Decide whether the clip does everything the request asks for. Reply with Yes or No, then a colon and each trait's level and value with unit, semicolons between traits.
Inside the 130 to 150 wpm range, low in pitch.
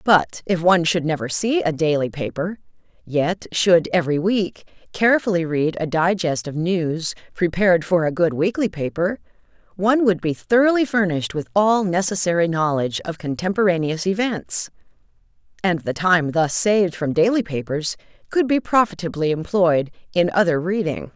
No: average, 145 wpm; medium, 175 Hz